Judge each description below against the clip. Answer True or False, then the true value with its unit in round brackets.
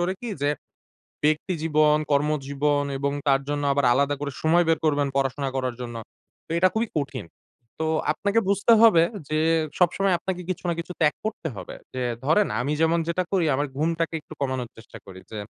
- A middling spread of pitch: True (3.5 semitones)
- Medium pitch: True (150 Hz)